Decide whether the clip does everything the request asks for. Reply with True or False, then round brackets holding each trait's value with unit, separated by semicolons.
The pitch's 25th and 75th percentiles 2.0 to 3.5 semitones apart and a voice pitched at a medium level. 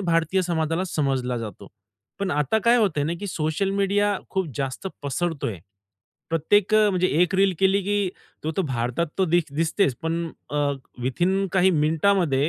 False (4.6 semitones; 170 Hz)